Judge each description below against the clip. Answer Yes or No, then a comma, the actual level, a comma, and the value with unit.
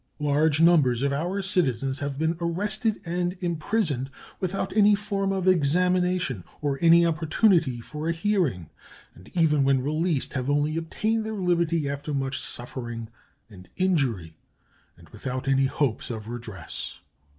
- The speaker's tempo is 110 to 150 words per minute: Yes, average, 140 wpm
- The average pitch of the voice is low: No, medium, 155 Hz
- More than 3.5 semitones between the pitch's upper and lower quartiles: Yes, average, 5.1 semitones